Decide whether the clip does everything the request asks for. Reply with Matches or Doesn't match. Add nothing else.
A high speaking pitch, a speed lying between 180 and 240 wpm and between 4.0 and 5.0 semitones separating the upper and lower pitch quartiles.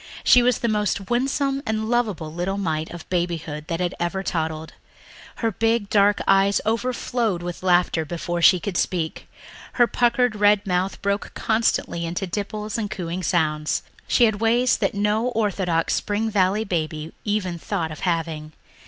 Doesn't match